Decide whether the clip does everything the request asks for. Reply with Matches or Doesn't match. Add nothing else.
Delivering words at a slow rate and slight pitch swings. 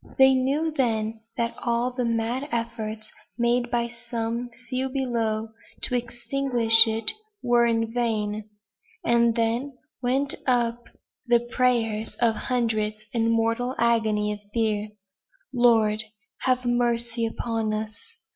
Matches